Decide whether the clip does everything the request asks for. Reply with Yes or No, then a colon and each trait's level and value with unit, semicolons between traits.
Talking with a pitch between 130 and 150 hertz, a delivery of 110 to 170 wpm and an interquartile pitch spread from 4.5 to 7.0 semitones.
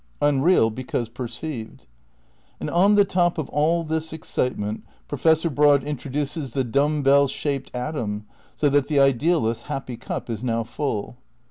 No: medium, 140 Hz; average, 155 wpm; average, 4.0 semitones